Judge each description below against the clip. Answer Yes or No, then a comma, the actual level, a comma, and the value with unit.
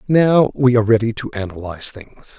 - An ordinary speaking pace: Yes, average, 175 wpm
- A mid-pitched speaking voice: No, low, 115 Hz